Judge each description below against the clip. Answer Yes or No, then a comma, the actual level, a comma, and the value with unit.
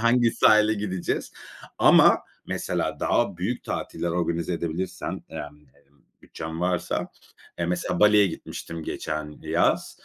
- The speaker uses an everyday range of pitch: Yes, average, 4.4 semitones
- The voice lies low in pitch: Yes, very low, 85 Hz